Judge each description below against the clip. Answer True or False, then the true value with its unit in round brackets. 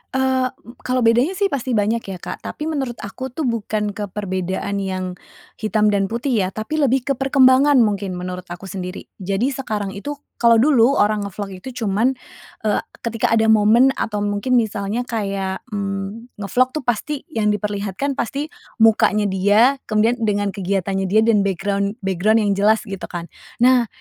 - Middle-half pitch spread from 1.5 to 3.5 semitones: False (3.9 semitones)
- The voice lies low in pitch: False (215 Hz)